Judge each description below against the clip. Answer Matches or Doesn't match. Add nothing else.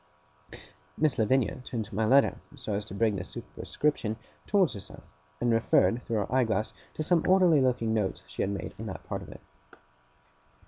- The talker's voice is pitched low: Matches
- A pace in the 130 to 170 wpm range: Doesn't match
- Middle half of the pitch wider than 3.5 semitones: Matches